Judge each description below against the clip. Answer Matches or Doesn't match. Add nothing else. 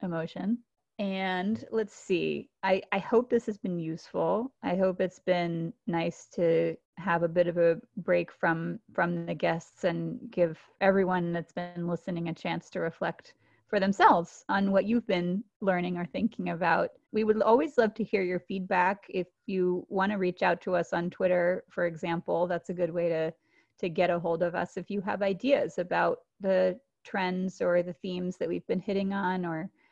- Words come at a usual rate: Matches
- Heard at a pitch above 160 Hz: Matches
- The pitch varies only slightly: Matches